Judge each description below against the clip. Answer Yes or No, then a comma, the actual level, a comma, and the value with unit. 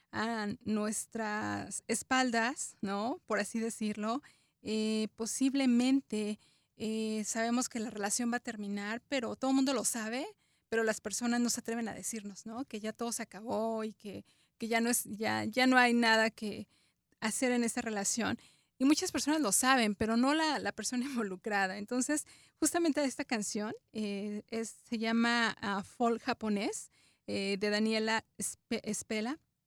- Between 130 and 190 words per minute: Yes, average, 160 wpm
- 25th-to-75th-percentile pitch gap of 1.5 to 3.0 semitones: Yes, narrow, 2.5 semitones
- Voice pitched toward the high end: Yes, high, 225 Hz